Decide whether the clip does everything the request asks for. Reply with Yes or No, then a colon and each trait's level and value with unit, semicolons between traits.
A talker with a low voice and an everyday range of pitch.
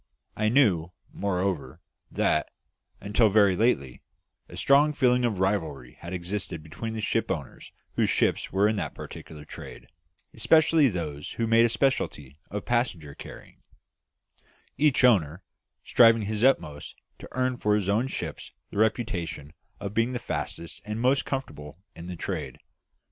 No: low, 105 Hz; wide, 6.0 semitones